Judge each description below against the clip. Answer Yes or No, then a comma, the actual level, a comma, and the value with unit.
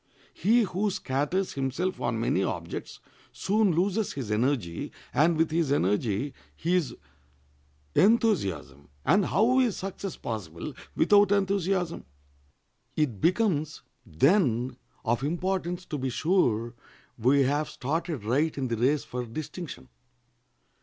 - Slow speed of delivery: Yes, slow, 115 wpm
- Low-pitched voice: No, medium, 150 Hz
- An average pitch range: No, wide, 7.6 semitones